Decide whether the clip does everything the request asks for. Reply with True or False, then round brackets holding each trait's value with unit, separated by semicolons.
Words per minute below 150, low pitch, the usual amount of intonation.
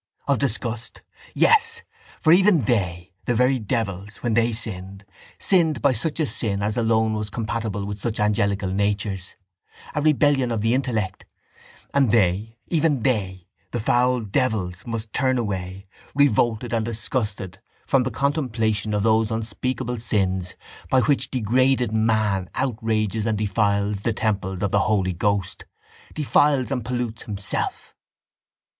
True (140 wpm; 110 Hz; 3.8 semitones)